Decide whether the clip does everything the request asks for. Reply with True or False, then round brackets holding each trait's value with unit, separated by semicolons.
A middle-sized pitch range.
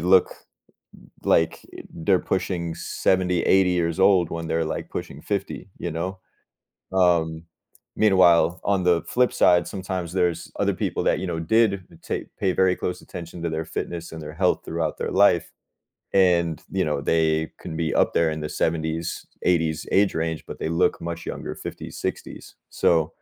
False (2.2 semitones)